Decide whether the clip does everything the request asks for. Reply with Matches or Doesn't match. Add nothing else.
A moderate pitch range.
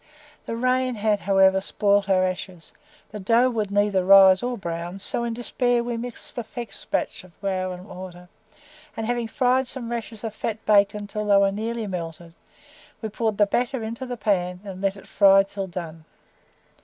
Matches